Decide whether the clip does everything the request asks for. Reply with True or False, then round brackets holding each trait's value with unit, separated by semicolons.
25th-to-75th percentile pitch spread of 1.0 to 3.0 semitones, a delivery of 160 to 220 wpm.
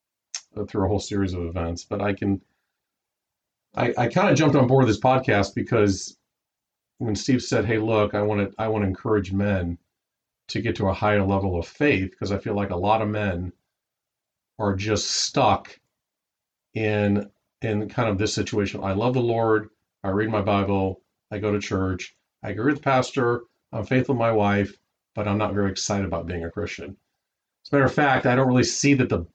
True (2.6 semitones; 200 wpm)